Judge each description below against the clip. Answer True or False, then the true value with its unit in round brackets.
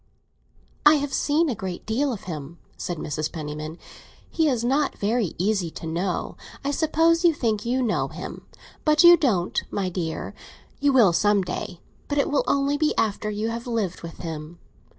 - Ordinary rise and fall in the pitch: False (8.4 semitones)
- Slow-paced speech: False (180 wpm)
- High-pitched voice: True (220 Hz)